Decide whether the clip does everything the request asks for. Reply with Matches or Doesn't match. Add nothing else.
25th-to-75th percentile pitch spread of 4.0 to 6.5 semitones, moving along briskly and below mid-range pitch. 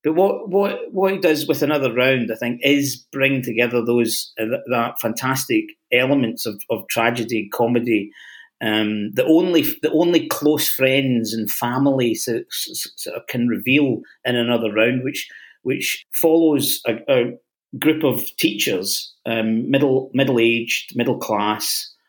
Doesn't match